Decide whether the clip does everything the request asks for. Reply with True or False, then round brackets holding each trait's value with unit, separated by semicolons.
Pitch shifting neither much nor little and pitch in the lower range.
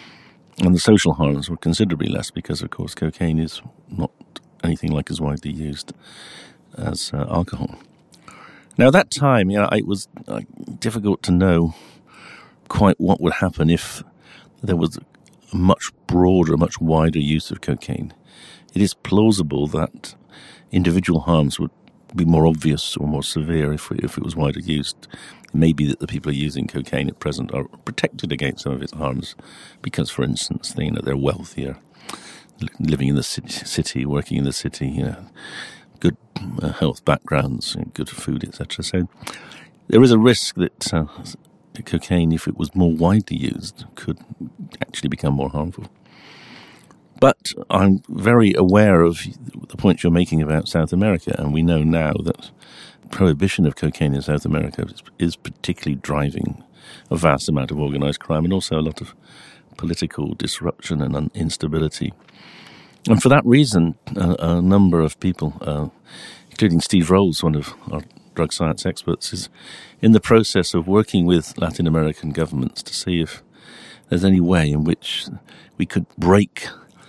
True (3.8 semitones; 80 Hz)